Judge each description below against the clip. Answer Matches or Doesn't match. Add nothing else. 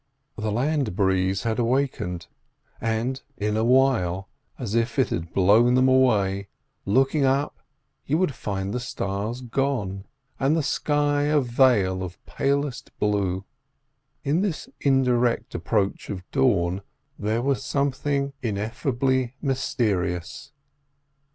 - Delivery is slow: Matches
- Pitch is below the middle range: Matches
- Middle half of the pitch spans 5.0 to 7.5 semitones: Matches